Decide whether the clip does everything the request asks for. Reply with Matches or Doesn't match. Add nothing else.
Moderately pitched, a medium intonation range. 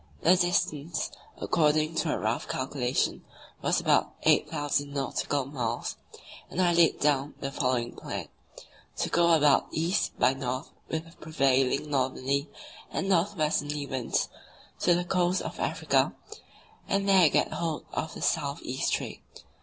Matches